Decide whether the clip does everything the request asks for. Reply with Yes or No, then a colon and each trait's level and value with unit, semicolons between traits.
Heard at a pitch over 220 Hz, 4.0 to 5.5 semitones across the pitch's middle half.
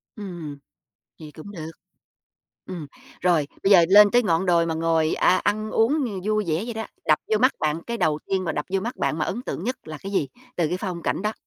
No: medium, 185 Hz; average, 4.7 semitones